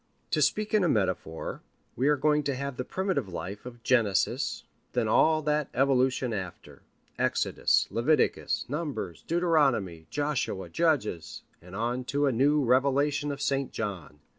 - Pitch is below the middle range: Yes, low, 130 Hz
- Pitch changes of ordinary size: No, wide, 5.8 semitones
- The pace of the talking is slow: No, average, 145 wpm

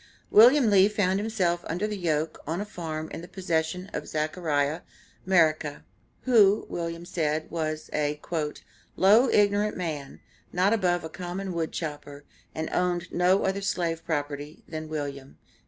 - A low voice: No, medium, 170 Hz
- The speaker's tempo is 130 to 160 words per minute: Yes, average, 145 wpm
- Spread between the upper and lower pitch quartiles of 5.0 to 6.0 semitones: No, average, 3.6 semitones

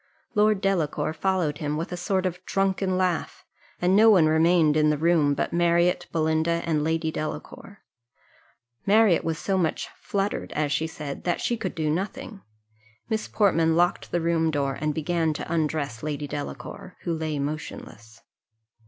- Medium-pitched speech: Yes, medium, 165 Hz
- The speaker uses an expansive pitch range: No, average, 3.3 semitones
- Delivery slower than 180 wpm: Yes, average, 160 wpm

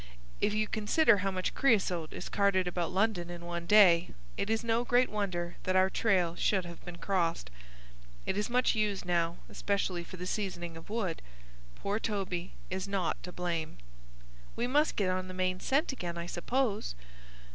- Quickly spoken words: No, average, 180 wpm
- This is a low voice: No, medium, 185 Hz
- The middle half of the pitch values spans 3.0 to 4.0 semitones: Yes, average, 3.4 semitones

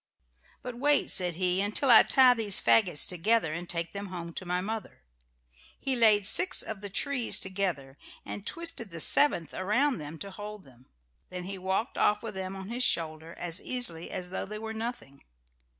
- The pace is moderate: Yes, average, 185 wpm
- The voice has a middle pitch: No, high, 195 Hz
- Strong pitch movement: No, average, 4.4 semitones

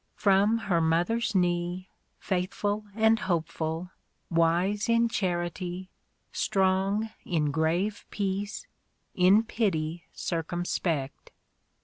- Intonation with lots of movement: No, average, 3.2 semitones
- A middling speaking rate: No, slow, 85 wpm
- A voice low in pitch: No, medium, 185 Hz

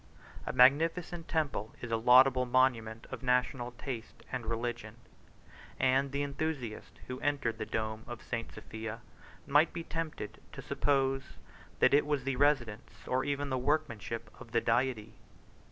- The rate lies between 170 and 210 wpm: No, average, 150 wpm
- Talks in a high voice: No, low, 130 Hz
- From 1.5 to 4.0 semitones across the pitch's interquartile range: Yes, average, 3.6 semitones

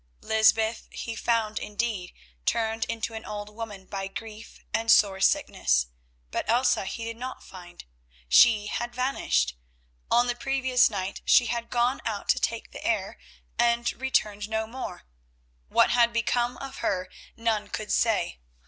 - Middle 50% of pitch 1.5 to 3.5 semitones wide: Yes, narrow, 2.5 semitones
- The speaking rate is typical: Yes, average, 150 wpm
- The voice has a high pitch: Yes, high, 225 Hz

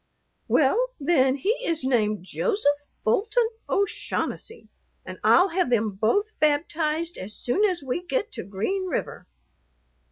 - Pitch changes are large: Yes, wide, 7.6 semitones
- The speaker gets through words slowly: Yes, slow, 130 wpm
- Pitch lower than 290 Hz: No, very high, 315 Hz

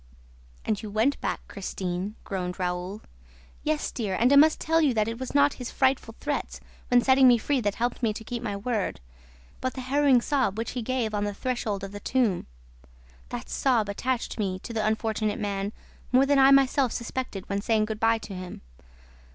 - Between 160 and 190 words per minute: No, average, 200 wpm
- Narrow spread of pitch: No, average, 4.2 semitones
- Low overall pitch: No, high, 225 Hz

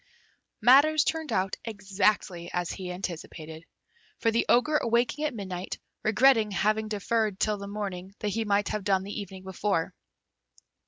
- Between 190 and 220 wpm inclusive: No, average, 150 wpm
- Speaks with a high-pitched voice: Yes, high, 205 Hz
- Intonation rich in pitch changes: No, average, 3.2 semitones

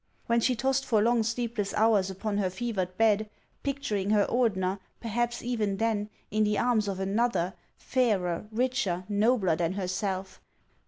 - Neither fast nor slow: Yes, average, 150 wpm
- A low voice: No, high, 215 Hz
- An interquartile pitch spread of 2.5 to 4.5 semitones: Yes, average, 3.6 semitones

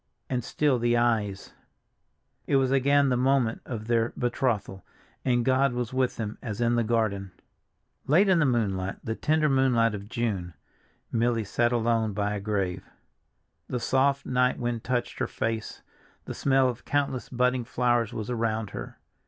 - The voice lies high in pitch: No, low, 120 Hz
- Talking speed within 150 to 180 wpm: Yes, average, 160 wpm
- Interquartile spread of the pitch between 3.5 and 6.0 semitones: No, average, 2.9 semitones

